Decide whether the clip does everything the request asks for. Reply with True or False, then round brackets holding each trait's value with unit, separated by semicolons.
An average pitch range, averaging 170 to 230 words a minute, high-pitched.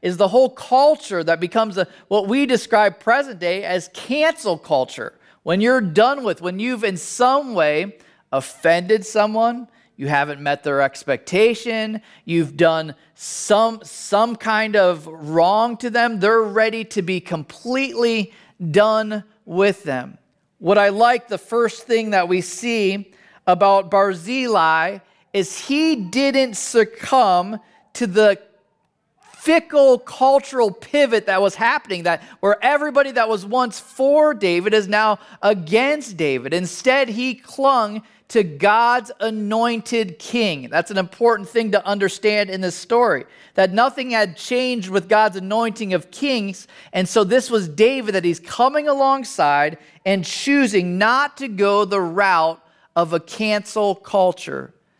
False (4.3 semitones; 140 wpm; 215 Hz)